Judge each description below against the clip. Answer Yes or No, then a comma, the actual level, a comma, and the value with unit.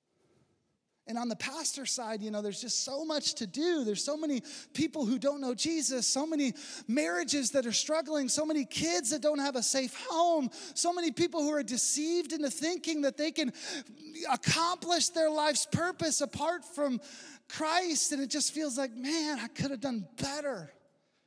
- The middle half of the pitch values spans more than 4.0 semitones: No, average, 3.0 semitones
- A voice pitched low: No, very high, 290 Hz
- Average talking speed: Yes, average, 185 wpm